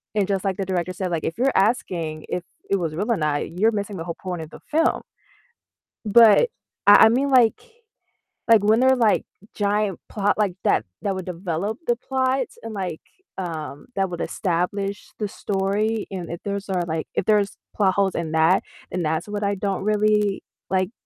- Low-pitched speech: No, high, 195 Hz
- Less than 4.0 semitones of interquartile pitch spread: Yes, average, 3.2 semitones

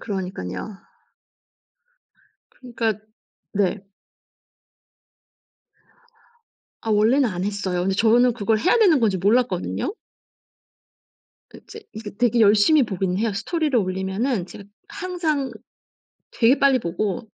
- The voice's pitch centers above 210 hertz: Yes, high, 220 Hz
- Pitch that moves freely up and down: No, average, 4.7 semitones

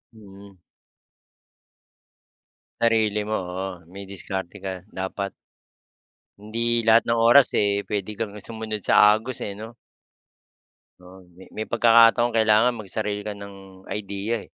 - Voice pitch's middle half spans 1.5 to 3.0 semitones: Yes, narrow, 2.4 semitones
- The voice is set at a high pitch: No, low, 105 Hz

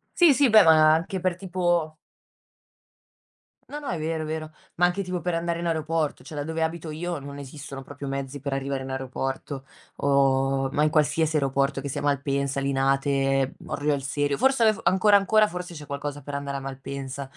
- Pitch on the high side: No, medium, 145 Hz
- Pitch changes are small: No, average, 3.6 semitones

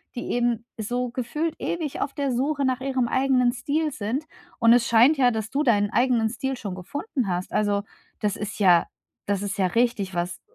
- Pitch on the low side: No, high, 240 Hz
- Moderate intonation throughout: Yes, average, 4.4 semitones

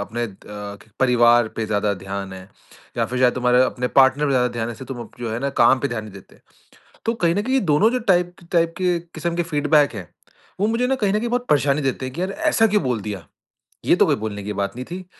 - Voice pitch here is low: Yes, low, 130 Hz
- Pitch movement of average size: No, wide, 7.7 semitones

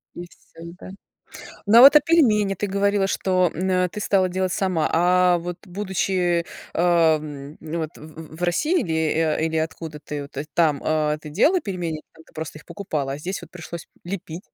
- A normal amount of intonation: Yes, average, 3.2 semitones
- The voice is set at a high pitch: No, medium, 175 Hz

